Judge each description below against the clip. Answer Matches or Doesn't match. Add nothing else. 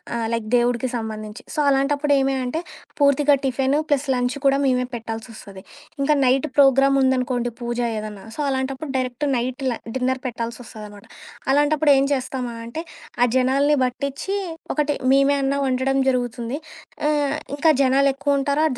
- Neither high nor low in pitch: Doesn't match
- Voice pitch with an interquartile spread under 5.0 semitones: Matches